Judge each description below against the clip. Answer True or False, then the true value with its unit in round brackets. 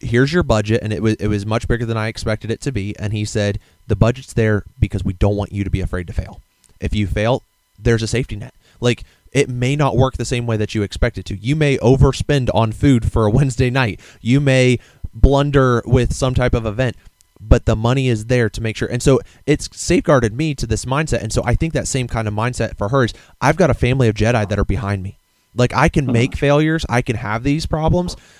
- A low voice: True (115 Hz)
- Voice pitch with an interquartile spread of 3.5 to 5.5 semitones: True (3.8 semitones)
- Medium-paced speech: False (245 wpm)